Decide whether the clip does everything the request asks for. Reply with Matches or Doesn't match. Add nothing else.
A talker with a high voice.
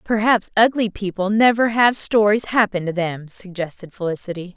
Matches